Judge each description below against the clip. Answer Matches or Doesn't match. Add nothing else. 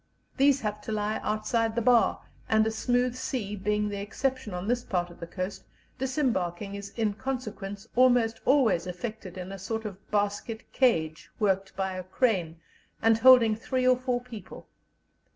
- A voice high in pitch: Matches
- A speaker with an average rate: Matches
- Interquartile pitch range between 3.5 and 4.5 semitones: Matches